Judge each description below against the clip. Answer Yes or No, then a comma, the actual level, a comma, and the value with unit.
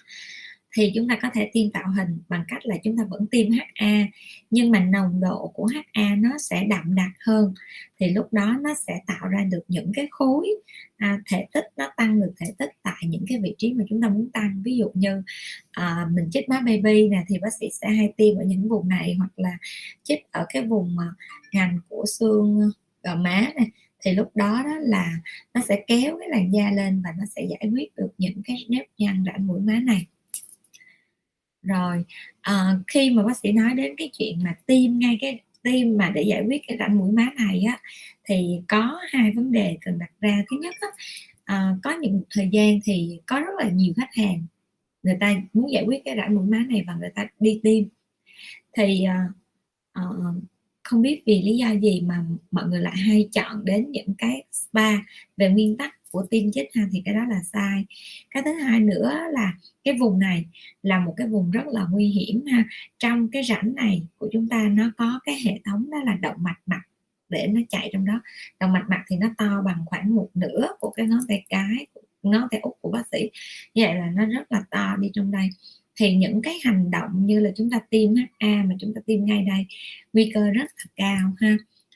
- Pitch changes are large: No, average, 3.0 semitones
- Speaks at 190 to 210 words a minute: No, average, 220 wpm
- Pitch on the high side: Yes, high, 210 Hz